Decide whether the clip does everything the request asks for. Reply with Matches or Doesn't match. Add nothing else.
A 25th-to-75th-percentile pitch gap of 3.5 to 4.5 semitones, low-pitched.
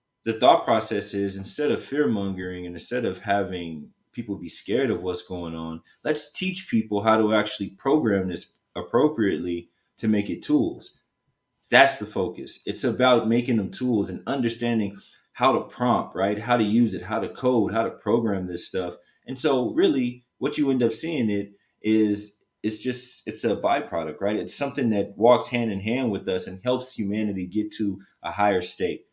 Matches